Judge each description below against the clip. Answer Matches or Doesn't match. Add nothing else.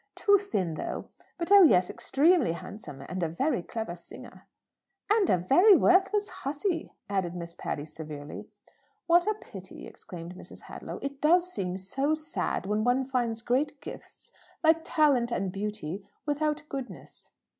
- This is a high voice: Matches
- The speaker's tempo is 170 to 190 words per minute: Doesn't match